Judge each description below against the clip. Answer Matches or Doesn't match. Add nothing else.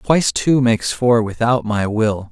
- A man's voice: Matches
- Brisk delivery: Doesn't match